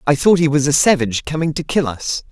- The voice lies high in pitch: No, medium, 145 Hz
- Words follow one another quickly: Yes, fast, 260 wpm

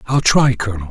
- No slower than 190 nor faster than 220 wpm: Yes, average, 200 wpm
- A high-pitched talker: No, low, 115 Hz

